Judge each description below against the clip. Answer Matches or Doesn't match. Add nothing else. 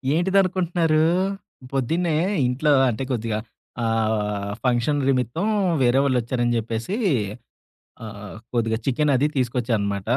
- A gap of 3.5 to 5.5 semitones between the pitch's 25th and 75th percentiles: Matches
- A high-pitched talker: Doesn't match